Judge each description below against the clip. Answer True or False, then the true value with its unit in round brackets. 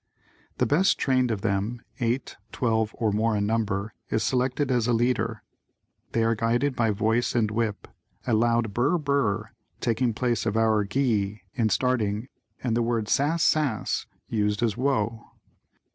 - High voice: False (115 Hz)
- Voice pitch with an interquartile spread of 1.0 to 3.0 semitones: True (2.6 semitones)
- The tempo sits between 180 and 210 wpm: False (165 wpm)